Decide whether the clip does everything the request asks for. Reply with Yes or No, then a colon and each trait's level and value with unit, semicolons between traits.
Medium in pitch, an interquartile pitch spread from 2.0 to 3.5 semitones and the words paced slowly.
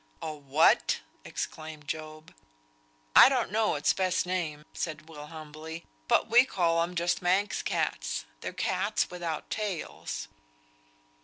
Yes: medium, 160 Hz; average, 2.9 semitones; slow, 130 wpm